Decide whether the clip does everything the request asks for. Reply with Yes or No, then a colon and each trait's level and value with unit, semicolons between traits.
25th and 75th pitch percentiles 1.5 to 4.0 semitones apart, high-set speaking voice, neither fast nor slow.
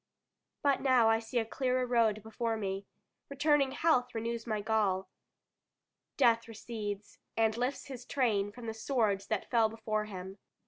Yes: average, 2.7 semitones; high, 225 Hz; average, 150 wpm